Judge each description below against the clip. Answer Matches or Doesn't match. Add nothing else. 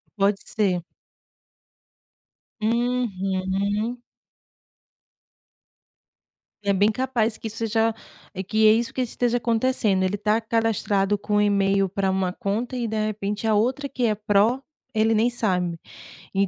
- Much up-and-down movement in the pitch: Doesn't match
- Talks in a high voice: Matches